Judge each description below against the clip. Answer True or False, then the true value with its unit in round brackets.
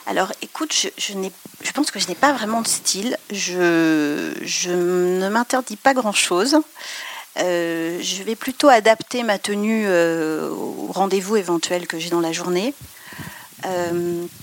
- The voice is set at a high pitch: True (195 Hz)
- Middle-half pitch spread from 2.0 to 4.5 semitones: False (5.6 semitones)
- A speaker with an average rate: True (155 wpm)